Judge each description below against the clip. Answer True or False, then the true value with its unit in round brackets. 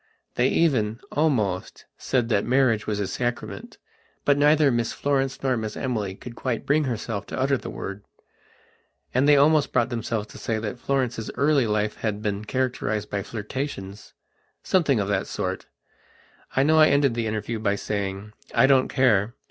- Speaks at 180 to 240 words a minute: False (165 wpm)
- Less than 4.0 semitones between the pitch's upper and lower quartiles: False (4.4 semitones)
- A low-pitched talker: True (120 Hz)